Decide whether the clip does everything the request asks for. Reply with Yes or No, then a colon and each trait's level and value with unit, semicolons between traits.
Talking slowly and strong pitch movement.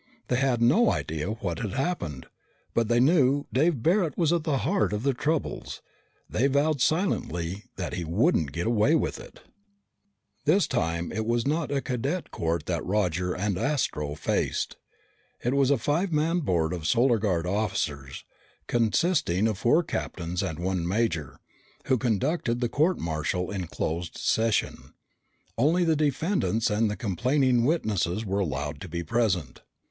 No: average, 160 wpm; wide, 8.2 semitones